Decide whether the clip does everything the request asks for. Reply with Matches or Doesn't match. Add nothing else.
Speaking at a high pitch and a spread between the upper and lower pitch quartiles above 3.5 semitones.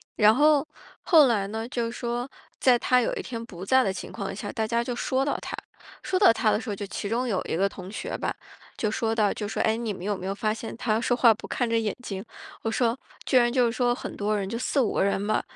Doesn't match